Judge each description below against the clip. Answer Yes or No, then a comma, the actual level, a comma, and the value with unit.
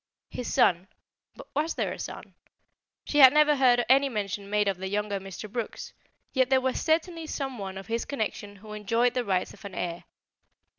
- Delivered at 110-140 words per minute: No, average, 195 wpm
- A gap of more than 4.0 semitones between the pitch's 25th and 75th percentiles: Yes, average, 5.0 semitones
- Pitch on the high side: Yes, high, 230 Hz